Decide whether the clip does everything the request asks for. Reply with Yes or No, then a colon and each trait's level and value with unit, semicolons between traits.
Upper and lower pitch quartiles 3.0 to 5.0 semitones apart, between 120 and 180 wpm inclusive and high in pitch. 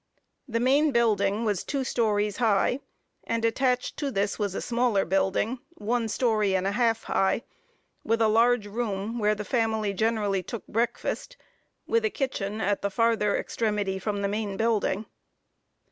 No: narrow, 2.6 semitones; average, 160 wpm; high, 220 Hz